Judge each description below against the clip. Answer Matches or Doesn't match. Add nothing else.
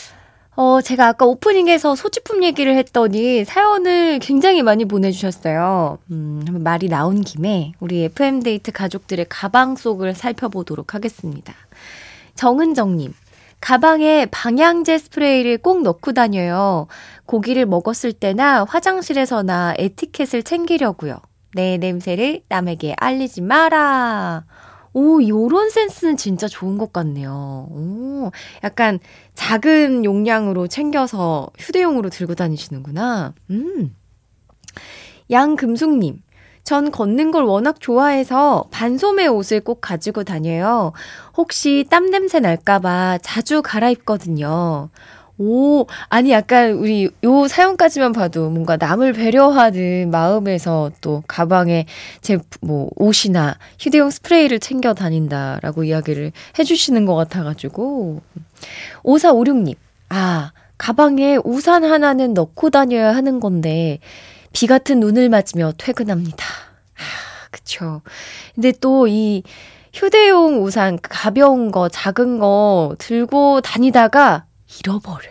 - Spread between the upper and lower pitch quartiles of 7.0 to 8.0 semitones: Matches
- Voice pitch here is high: Matches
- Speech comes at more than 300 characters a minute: Doesn't match